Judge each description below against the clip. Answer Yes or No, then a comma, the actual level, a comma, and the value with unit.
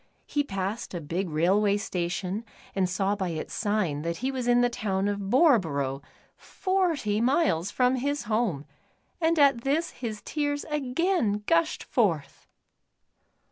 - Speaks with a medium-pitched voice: No, high, 210 Hz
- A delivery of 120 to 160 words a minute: Yes, average, 140 wpm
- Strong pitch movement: Yes, wide, 6.7 semitones